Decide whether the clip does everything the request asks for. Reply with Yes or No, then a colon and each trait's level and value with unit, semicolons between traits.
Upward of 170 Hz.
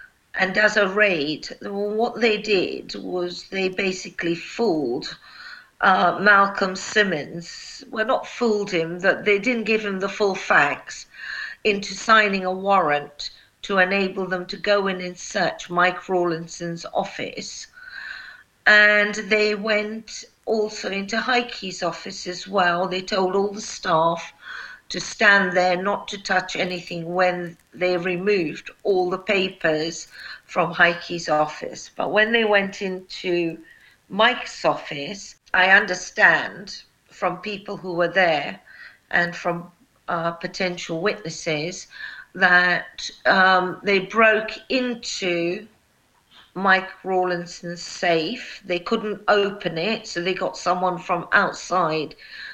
Yes: high, 190 Hz